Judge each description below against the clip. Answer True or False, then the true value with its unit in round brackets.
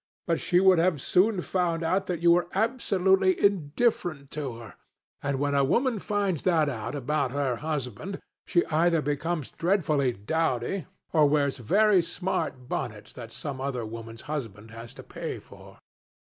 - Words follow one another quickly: False (160 wpm)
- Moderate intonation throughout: False (5.7 semitones)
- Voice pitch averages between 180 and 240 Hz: False (155 Hz)